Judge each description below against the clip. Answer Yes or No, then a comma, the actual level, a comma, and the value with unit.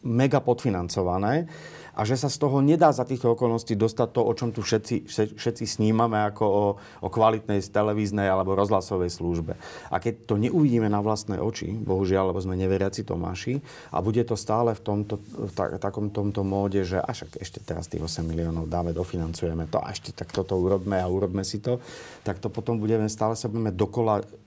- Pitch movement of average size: Yes, average, 3.3 semitones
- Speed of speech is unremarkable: No, fast, 190 wpm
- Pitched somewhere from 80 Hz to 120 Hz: Yes, low, 105 Hz